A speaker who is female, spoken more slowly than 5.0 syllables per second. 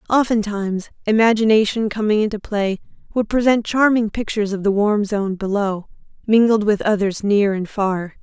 No: female; 5.1 syllables/s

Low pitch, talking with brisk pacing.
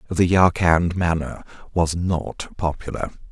No: very low, 85 Hz; slow, 110 wpm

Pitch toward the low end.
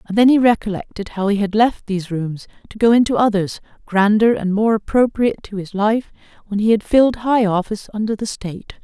No: high, 210 Hz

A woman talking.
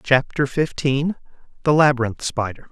No: male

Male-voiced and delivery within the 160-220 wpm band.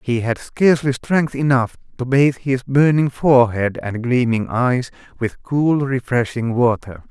No: male; average, 145 wpm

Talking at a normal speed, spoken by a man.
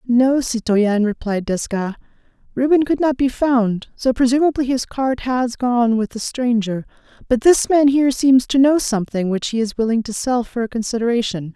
No: average, 180 wpm; female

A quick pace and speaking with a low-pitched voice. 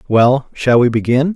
No: average, 175 wpm; low, 130 Hz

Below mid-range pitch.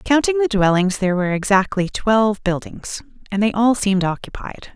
No: high, 205 Hz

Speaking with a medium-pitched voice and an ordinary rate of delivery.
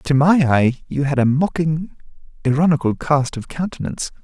Yes: medium, 150 Hz; average, 155 wpm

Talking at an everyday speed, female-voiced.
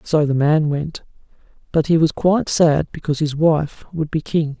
No: average, 195 wpm; male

